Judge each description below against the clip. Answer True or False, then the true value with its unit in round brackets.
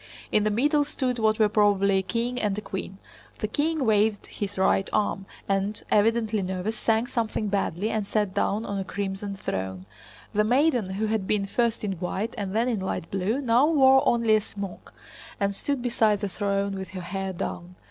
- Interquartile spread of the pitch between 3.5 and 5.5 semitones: False (2.7 semitones)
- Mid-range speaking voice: False (210 Hz)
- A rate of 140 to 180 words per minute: False (195 wpm)